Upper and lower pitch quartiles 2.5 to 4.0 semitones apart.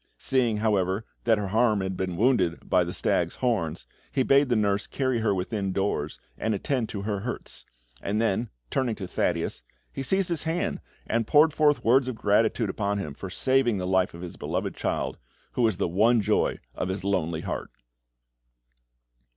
No: average, 4.5 semitones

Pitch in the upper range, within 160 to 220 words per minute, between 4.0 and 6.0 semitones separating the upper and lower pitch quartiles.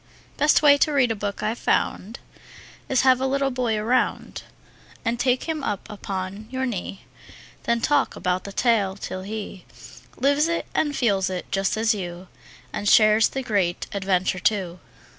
Yes: high, 220 Hz; average, 165 wpm; average, 5.1 semitones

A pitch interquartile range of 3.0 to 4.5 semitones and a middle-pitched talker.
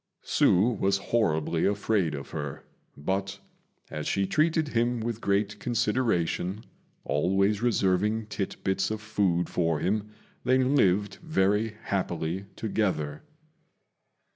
No: average, 3.6 semitones; low, 100 Hz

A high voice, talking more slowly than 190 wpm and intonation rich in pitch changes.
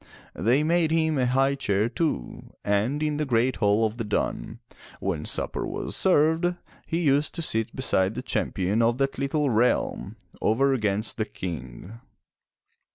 No: low, 125 Hz; average, 160 wpm; wide, 5.9 semitones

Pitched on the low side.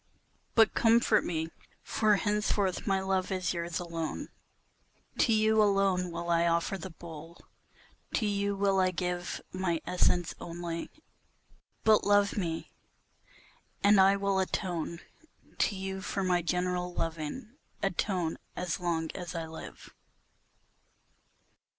No: medium, 185 Hz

